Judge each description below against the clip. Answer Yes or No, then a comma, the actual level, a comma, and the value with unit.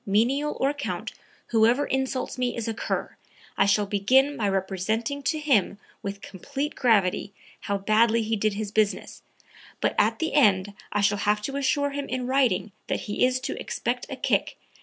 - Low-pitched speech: No, high, 225 Hz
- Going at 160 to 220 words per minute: Yes, average, 180 wpm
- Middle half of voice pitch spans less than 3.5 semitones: No, average, 4.8 semitones